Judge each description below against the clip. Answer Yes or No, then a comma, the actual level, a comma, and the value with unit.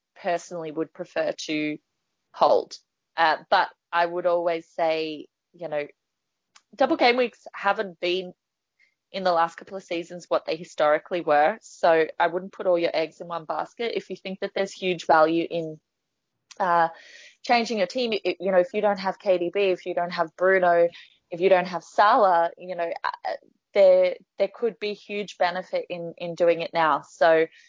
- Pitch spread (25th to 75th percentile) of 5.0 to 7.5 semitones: No, average, 2.7 semitones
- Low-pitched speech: No, medium, 180 Hz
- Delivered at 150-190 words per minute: Yes, average, 180 wpm